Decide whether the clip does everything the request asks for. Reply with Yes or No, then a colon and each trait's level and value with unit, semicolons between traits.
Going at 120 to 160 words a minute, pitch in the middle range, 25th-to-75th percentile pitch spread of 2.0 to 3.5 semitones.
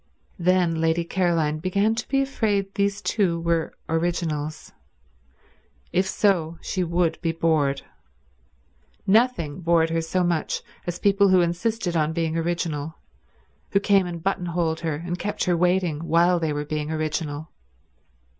Yes: average, 140 wpm; medium, 170 Hz; narrow, 2.5 semitones